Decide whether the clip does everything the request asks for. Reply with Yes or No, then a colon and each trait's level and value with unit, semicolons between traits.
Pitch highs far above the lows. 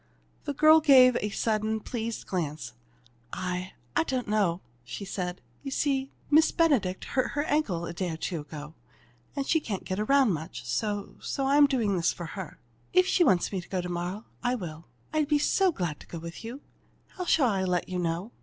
Yes: wide, 7.5 semitones